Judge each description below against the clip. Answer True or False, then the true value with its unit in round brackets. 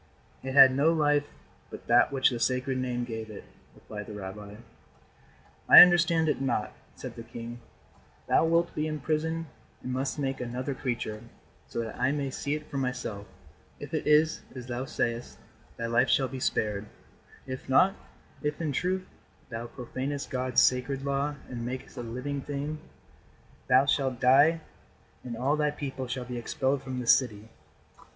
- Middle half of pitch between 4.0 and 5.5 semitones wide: False (3.2 semitones)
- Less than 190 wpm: True (165 wpm)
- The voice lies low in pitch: True (130 Hz)